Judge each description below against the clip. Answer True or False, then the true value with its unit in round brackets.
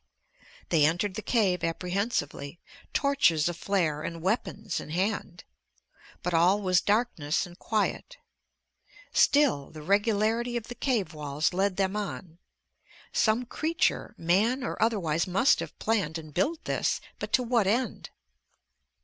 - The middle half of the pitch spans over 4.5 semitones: True (5.3 semitones)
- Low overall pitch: False (195 Hz)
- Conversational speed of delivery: False (130 wpm)